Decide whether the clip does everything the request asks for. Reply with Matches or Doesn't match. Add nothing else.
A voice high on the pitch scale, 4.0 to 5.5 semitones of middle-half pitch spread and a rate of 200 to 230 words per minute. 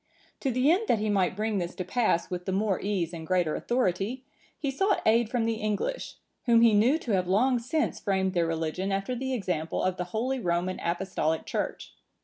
Matches